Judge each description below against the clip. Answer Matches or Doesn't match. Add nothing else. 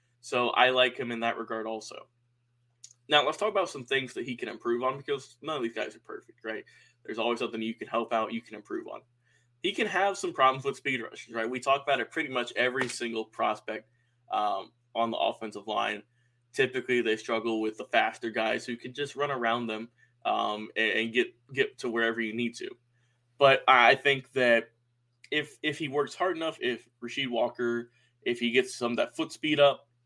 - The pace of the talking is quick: Matches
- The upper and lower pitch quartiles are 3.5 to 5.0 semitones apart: Doesn't match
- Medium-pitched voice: Doesn't match